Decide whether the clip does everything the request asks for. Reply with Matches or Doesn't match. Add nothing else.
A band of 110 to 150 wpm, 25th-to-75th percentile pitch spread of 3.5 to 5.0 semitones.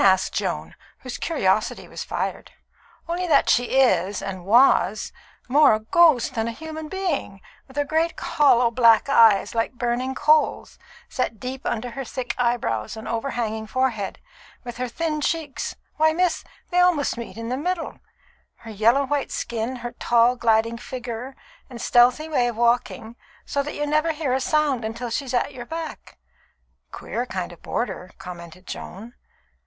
Doesn't match